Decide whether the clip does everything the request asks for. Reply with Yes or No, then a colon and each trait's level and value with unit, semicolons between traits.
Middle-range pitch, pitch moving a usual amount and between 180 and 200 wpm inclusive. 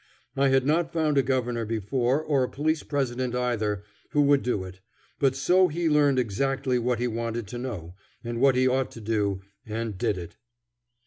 No: low, 125 Hz; average, 3.4 semitones; average, 190 wpm